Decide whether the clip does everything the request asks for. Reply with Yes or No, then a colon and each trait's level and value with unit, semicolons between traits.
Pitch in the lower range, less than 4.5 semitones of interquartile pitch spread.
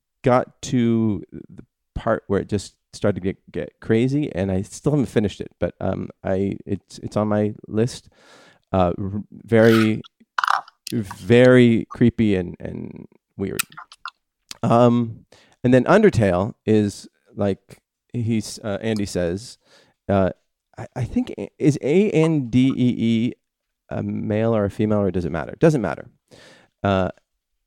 Yes: low, 110 Hz; average, 3.3 semitones